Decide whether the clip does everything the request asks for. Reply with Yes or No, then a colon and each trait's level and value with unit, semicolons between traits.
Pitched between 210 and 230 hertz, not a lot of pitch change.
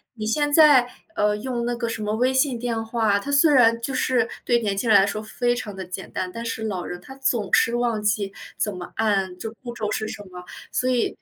No: high, 225 Hz; average, 3.0 semitones